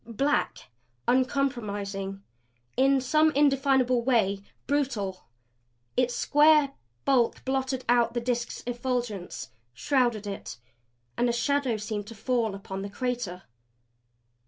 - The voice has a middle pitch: No, high, 245 Hz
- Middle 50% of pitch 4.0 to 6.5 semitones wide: Yes, average, 4.3 semitones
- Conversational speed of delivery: No, slow, 110 wpm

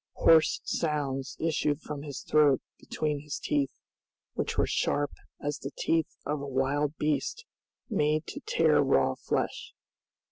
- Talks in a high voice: No, medium, 150 Hz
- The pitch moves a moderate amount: No, narrow, 1.6 semitones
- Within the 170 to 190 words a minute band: No, average, 140 wpm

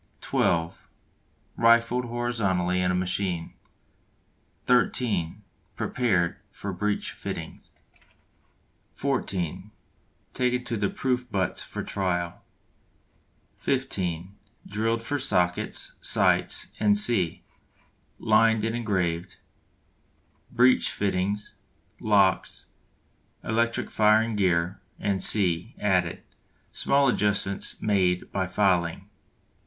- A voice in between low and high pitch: No, low, 100 Hz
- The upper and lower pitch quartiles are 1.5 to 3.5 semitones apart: No, average, 4.3 semitones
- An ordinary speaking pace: No, slow, 85 wpm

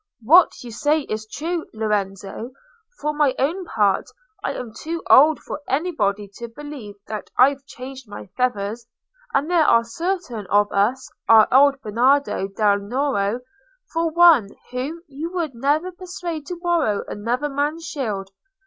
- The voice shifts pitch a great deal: Yes, wide, 6.3 semitones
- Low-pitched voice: No, very high, 265 Hz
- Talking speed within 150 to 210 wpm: No, average, 140 wpm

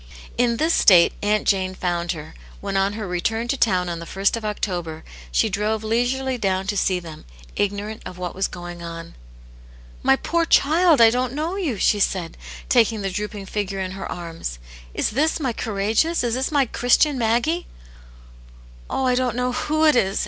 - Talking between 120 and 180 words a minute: No, average, 190 wpm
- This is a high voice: Yes, high, 210 Hz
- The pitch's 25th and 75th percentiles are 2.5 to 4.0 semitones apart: No, average, 5.3 semitones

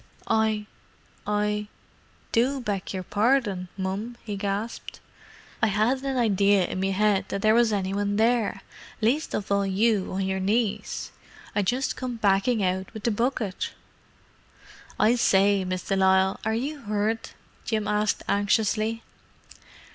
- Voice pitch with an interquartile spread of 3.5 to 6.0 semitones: No, average, 2.7 semitones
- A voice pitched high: Yes, high, 210 Hz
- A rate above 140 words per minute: No, slow, 135 wpm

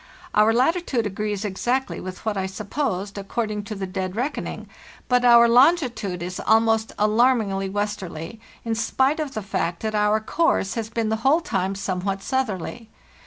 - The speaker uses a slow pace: No, average, 160 wpm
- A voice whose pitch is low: No, high, 215 Hz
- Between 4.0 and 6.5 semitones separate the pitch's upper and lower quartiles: No, average, 3.6 semitones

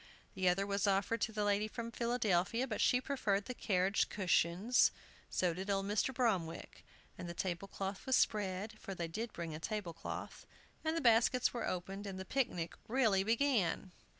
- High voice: Yes, high, 200 Hz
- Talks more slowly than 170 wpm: No, average, 180 wpm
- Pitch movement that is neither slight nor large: Yes, average, 3.9 semitones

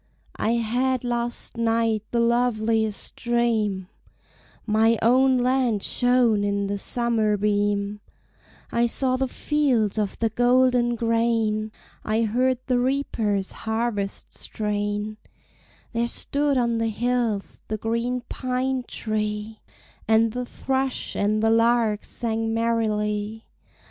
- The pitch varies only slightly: Yes, narrow, 2.3 semitones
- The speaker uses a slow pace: Yes, slow, 115 wpm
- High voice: Yes, high, 230 Hz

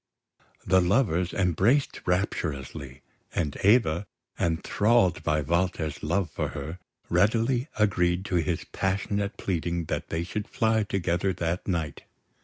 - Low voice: Yes, very low, 90 Hz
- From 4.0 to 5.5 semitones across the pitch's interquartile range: No, average, 3.5 semitones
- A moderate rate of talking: No, slow, 120 wpm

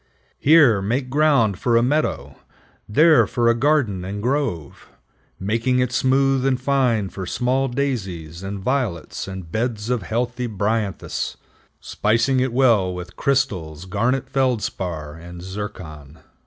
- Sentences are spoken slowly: Yes, slow, 130 wpm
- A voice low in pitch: Yes, low, 115 Hz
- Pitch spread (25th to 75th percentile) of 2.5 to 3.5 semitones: No, wide, 5.6 semitones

